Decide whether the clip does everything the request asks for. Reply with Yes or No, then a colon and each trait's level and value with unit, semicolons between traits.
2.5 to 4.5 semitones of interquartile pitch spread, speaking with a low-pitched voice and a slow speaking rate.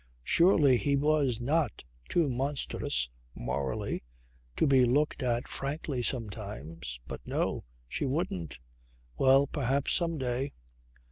Yes: average, 3.9 semitones; low, 130 Hz; slow, 115 wpm